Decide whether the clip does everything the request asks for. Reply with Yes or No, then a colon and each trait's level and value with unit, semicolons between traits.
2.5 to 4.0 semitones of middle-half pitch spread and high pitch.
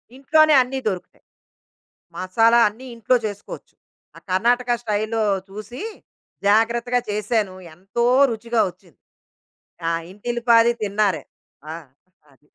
Yes: average, 2.8 semitones; high, 225 Hz